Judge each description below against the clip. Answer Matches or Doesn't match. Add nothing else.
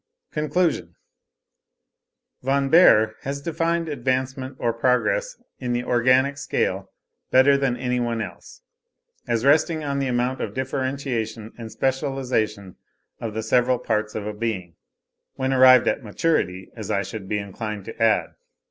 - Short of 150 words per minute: Matches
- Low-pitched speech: Matches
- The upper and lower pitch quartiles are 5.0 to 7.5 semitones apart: Doesn't match